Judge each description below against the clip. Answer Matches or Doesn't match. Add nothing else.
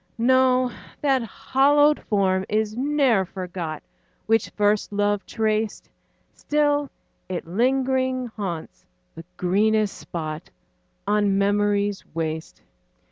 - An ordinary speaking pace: Doesn't match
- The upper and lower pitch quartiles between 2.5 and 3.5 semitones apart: Doesn't match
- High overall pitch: Matches